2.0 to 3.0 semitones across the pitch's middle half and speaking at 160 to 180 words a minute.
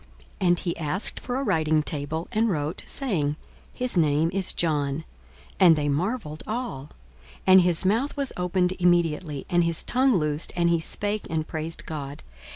No: average, 4.1 semitones; average, 170 wpm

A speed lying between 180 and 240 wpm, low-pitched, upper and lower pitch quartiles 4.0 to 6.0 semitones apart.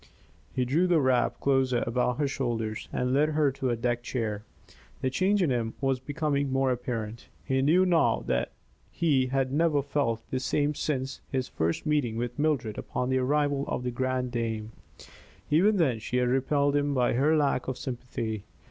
No: average, 185 wpm; low, 130 Hz; average, 3.0 semitones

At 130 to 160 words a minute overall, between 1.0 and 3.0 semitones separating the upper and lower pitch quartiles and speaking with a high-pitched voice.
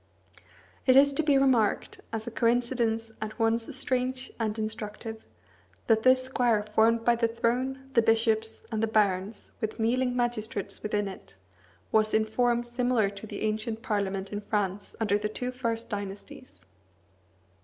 Yes: average, 155 wpm; narrow, 2.4 semitones; high, 225 Hz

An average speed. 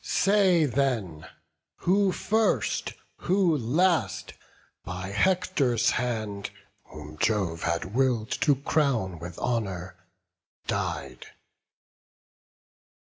No: slow, 80 wpm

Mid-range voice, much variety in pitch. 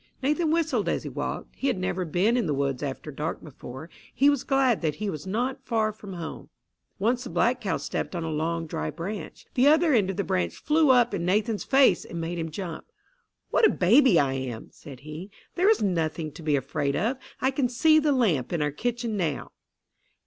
No: high, 195 Hz; wide, 8.3 semitones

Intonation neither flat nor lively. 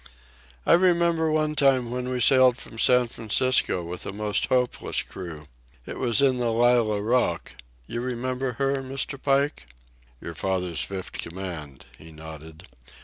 No: wide, 6.4 semitones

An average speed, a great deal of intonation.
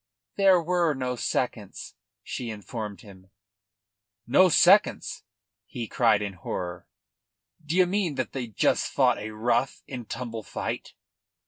No: slow, 125 wpm; wide, 7.4 semitones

